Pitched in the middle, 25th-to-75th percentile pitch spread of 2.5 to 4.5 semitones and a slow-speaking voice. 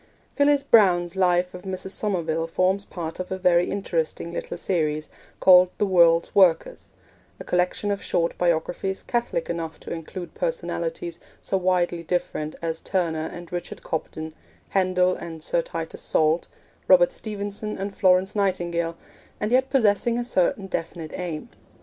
No: medium, 180 Hz; average, 3.0 semitones; average, 145 wpm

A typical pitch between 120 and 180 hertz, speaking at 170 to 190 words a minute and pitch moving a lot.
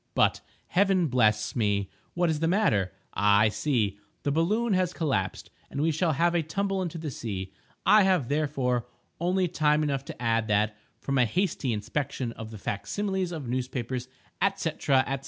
Yes: medium, 140 Hz; average, 175 wpm; wide, 7.4 semitones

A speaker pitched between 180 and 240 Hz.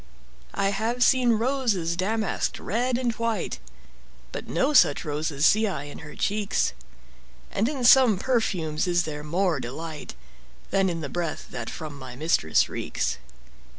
Yes: medium, 185 Hz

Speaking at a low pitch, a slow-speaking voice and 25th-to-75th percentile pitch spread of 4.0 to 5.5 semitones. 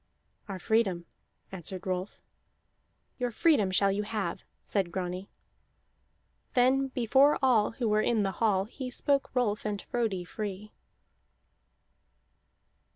No: high, 210 Hz; slow, 115 wpm; average, 4.3 semitones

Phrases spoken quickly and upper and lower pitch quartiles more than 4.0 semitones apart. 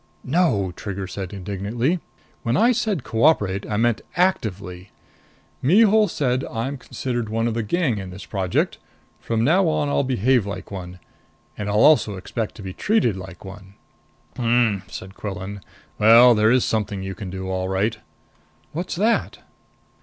No: average, 155 wpm; average, 5.3 semitones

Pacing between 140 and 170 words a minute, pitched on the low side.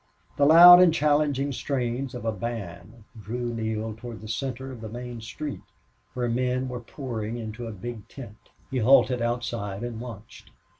Yes: average, 165 wpm; low, 120 Hz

